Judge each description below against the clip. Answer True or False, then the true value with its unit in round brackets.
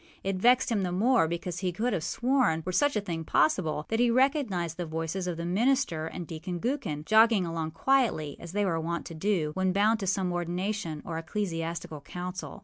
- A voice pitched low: False (180 Hz)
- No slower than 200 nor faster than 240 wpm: True (205 wpm)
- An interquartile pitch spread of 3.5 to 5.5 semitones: True (4.7 semitones)